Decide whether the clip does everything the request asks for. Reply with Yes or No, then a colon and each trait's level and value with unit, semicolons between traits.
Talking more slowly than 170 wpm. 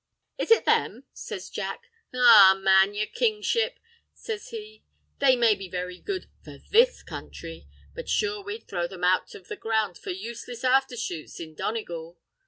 Yes: average, 160 wpm